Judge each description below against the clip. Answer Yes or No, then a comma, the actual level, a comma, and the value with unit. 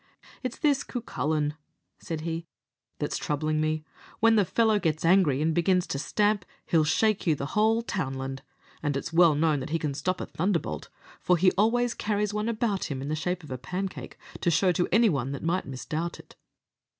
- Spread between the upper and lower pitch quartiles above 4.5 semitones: Yes, average, 5.3 semitones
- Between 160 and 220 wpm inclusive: Yes, average, 190 wpm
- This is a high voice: No, medium, 170 Hz